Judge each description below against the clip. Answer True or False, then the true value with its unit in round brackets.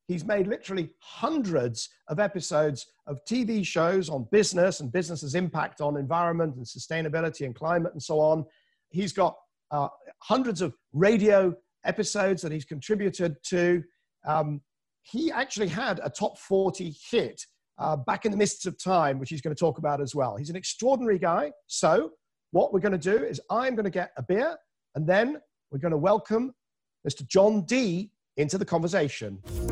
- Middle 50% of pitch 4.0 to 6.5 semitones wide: True (5.2 semitones)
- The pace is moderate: True (175 wpm)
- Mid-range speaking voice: True (175 Hz)